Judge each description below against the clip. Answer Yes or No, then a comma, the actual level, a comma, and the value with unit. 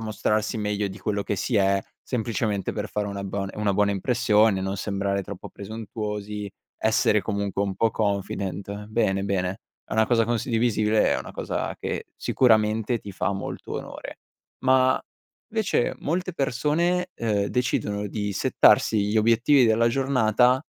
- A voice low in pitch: Yes, low, 105 Hz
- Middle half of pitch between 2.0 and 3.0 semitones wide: Yes, average, 2.7 semitones